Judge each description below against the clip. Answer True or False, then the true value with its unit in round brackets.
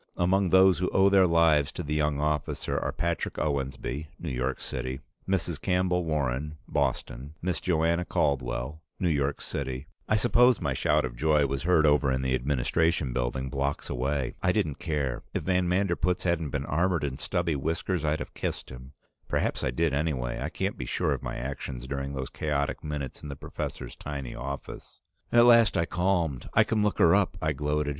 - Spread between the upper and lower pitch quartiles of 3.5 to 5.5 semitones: True (4.3 semitones)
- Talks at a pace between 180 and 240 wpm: True (190 wpm)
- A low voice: True (75 Hz)